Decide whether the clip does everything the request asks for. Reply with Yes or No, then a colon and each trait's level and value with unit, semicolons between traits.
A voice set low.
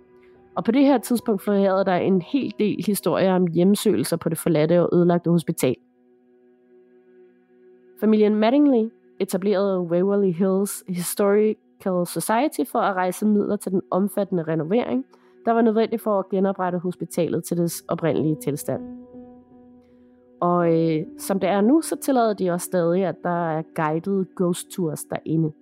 No: medium, 180 Hz